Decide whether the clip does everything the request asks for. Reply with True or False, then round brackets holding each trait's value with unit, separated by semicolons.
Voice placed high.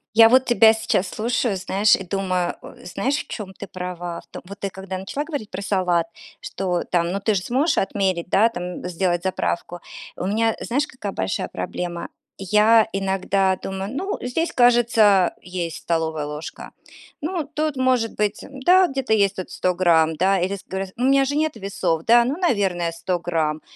True (195 Hz)